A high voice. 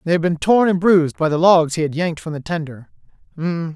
No: medium, 165 Hz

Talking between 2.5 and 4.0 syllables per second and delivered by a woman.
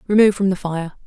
No: 7.2 syllables/s; female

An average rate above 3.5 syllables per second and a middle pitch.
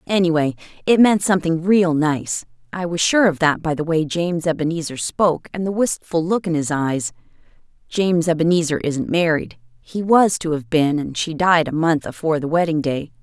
Yes: 5.3 syllables/s; medium, 165 Hz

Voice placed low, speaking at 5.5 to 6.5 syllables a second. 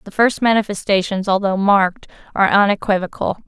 No: high, 200 Hz; 5.9 syllables/s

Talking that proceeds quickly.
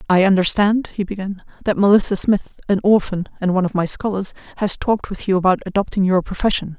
No: average, 195 wpm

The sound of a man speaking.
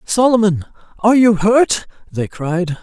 Yes: male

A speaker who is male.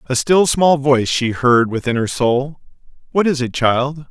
Yes: male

